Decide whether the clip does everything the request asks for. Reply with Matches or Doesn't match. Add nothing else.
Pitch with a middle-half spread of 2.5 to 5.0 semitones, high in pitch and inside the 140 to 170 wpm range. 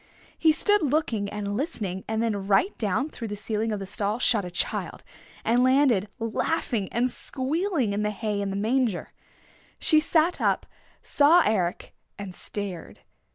Doesn't match